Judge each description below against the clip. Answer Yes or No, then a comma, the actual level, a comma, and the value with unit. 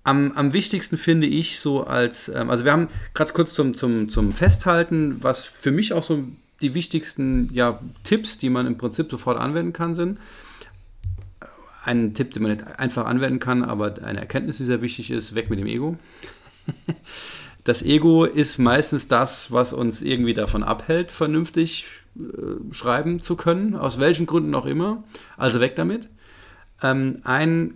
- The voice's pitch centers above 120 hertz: Yes, low, 135 Hz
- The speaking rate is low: No, average, 165 wpm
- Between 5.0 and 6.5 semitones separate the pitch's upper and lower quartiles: Yes, average, 5.3 semitones